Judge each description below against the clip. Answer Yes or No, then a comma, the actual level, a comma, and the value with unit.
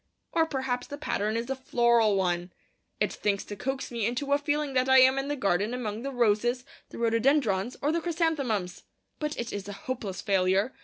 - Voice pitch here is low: No, high, 240 Hz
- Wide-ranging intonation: No, average, 4.8 semitones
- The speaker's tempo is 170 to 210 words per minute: Yes, average, 200 wpm